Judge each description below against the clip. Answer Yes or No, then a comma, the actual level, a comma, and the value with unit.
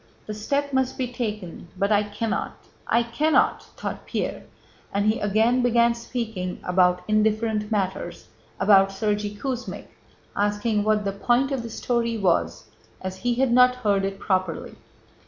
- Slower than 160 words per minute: Yes, average, 150 wpm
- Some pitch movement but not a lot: Yes, average, 3.2 semitones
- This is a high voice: Yes, high, 215 Hz